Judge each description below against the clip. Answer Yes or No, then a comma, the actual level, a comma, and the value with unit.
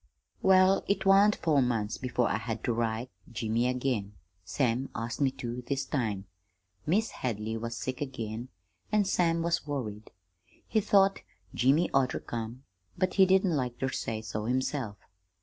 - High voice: No, low, 125 Hz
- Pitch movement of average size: No, wide, 6.6 semitones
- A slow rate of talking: No, average, 165 wpm